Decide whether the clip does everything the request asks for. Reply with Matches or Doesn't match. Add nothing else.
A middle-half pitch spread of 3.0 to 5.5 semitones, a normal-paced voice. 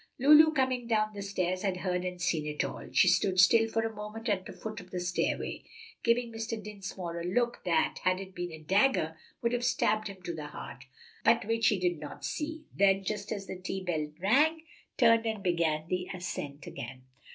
Doesn't match